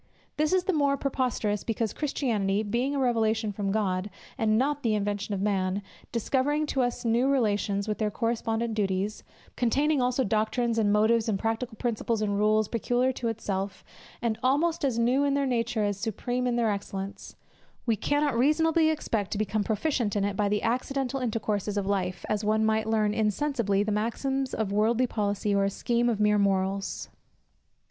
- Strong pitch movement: No, average, 3.5 semitones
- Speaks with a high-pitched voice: Yes, high, 220 Hz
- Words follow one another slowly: No, average, 180 wpm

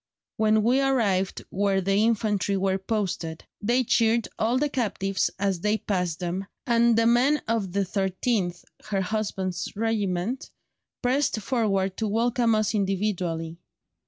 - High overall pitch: Yes, high, 205 Hz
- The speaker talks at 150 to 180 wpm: No, slow, 135 wpm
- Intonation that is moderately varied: Yes, average, 3.2 semitones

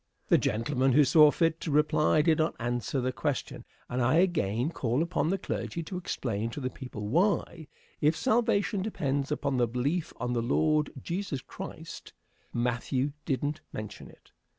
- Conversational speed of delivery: Yes, average, 160 wpm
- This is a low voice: No, medium, 145 Hz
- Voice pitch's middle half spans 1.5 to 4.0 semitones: No, average, 4.8 semitones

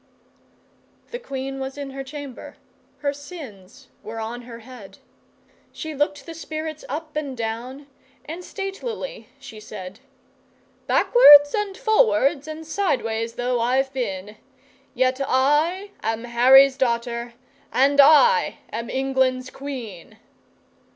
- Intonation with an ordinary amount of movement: Yes, average, 4.5 semitones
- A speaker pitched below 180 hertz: No, very high, 270 Hz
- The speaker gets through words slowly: Yes, slow, 115 wpm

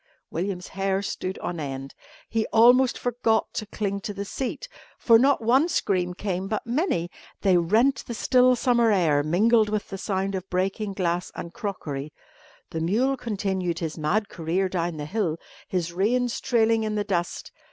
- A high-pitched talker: Yes, high, 200 Hz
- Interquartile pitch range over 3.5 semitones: Yes, average, 4.4 semitones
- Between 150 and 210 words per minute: Yes, average, 170 wpm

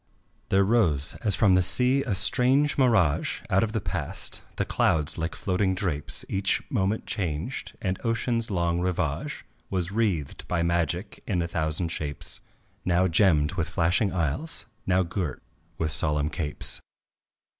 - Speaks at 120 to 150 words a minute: Yes, average, 145 wpm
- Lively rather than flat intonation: No, average, 4.1 semitones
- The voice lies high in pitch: No, very low, 90 Hz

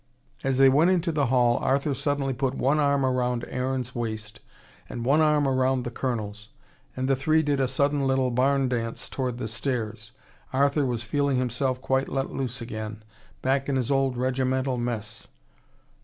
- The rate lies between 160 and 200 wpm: Yes, average, 170 wpm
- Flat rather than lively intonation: Yes, narrow, 2.2 semitones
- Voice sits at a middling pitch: No, low, 130 Hz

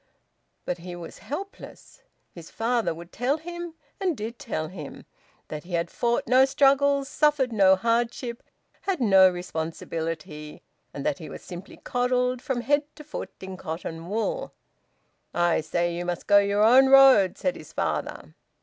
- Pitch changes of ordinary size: No, wide, 7.6 semitones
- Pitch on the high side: Yes, high, 220 Hz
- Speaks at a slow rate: No, average, 160 wpm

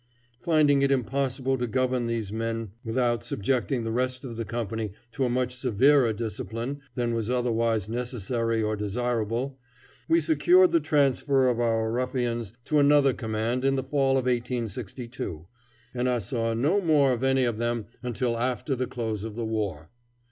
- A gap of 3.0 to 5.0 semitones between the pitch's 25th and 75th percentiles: No, narrow, 2.6 semitones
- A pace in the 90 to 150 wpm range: No, average, 165 wpm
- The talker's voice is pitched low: Yes, low, 120 Hz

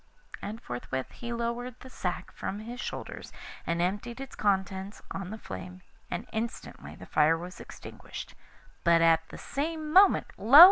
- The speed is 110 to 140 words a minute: No, average, 155 wpm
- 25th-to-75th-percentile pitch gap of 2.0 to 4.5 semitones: No, average, 5.1 semitones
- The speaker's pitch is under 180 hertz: No, high, 205 Hz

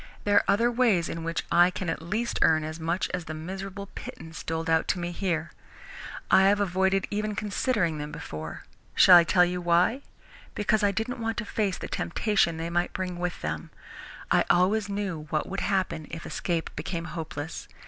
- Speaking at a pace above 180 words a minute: Yes, average, 190 wpm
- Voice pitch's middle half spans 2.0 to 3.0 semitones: No, average, 3.7 semitones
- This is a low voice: No, medium, 180 Hz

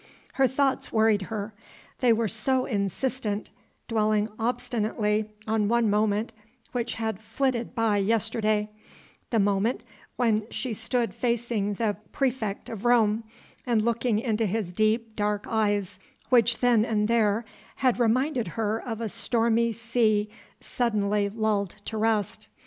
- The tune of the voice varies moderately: No, narrow, 2.0 semitones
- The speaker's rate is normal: No, slow, 130 wpm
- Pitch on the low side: No, high, 220 Hz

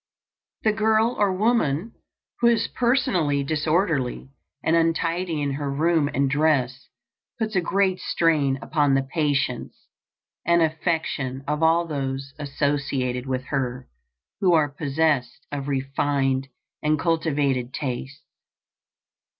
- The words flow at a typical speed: No, slow, 120 wpm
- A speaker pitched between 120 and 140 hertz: No, medium, 150 Hz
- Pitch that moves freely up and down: No, average, 3.7 semitones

